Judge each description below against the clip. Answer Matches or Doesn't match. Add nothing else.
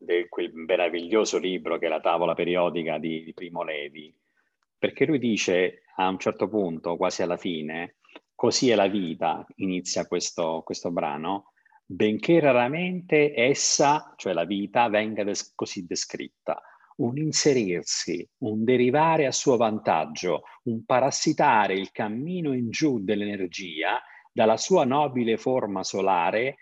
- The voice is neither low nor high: Doesn't match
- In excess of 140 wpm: Doesn't match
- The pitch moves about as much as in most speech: Doesn't match